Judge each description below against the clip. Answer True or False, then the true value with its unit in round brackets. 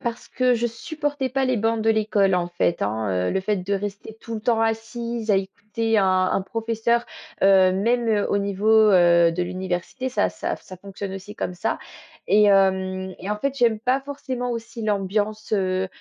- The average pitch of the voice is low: False (210 Hz)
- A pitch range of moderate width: True (3.3 semitones)